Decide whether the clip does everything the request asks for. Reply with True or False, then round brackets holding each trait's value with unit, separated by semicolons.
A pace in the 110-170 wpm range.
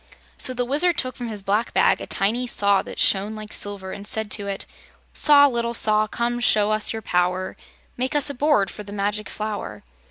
False (200 wpm)